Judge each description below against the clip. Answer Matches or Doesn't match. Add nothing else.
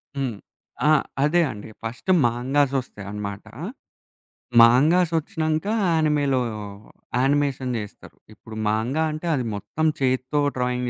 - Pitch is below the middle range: Matches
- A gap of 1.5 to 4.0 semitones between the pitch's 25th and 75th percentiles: Doesn't match